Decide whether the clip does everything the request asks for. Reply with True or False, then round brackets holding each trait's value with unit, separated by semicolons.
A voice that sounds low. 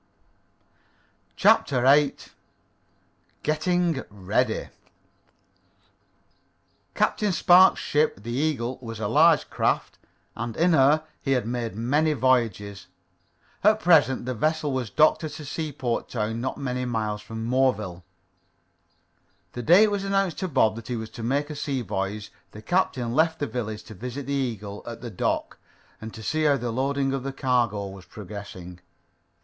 True (125 Hz)